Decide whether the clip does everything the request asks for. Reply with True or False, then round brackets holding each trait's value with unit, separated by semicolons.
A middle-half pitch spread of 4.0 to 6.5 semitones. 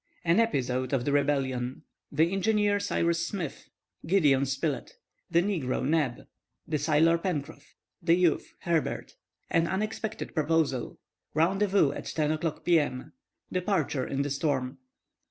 True (4.5 semitones)